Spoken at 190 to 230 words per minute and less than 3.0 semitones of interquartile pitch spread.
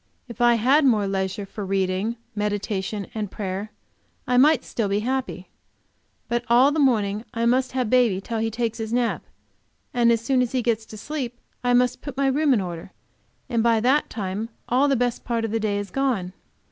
No: average, 200 wpm; average, 3.4 semitones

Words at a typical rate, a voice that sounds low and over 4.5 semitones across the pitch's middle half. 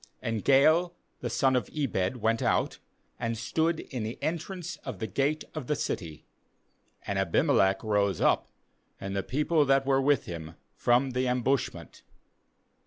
Yes: average, 155 wpm; low, 125 Hz; average, 5.2 semitones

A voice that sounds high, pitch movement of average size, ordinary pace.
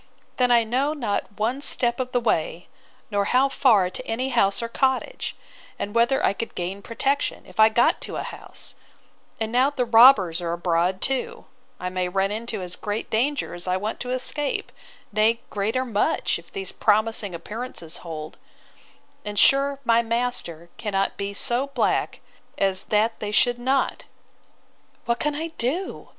Yes: high, 225 Hz; average, 4.5 semitones; average, 165 wpm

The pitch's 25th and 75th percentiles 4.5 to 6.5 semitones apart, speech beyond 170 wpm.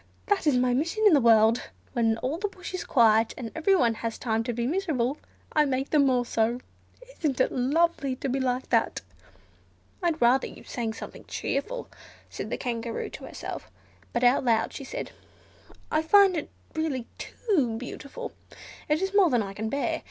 Yes: average, 5.3 semitones; average, 180 wpm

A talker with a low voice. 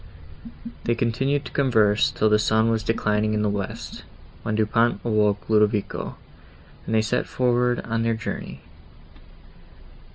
Yes: low, 110 Hz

